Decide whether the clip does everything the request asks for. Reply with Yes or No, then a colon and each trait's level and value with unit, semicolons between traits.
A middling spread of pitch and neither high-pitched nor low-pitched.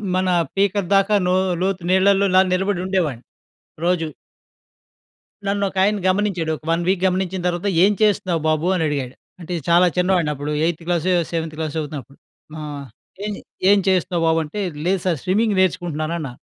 Yes: average, 3.1 semitones; medium, 180 Hz